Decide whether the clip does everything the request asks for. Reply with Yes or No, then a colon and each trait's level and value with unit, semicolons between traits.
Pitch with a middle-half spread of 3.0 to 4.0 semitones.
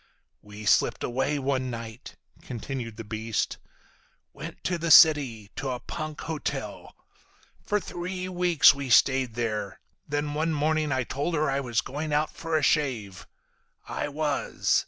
No: average, 4.6 semitones